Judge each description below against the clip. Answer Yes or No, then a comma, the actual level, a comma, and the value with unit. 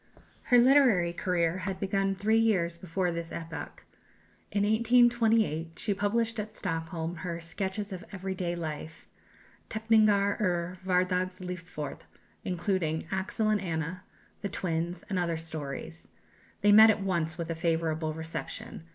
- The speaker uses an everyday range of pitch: Yes, average, 3.6 semitones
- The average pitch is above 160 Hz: Yes, medium, 185 Hz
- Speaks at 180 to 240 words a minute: No, slow, 135 wpm